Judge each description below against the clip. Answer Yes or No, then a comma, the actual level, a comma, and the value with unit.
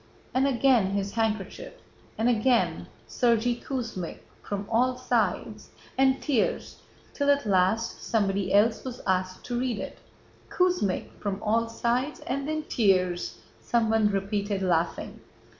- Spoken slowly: Yes, slow, 125 wpm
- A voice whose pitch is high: Yes, high, 225 Hz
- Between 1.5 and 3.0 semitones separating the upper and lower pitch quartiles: No, average, 4.2 semitones